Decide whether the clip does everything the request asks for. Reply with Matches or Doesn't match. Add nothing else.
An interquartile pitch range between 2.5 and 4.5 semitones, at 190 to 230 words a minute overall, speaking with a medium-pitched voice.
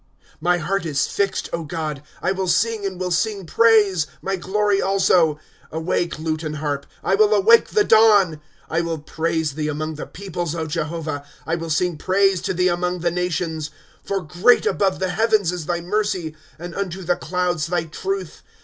Matches